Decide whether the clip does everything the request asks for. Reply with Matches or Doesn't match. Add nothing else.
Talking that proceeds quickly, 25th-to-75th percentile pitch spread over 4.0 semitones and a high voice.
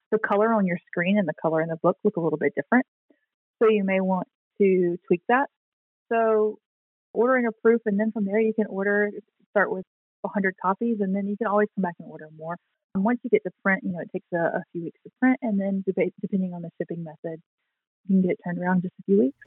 Doesn't match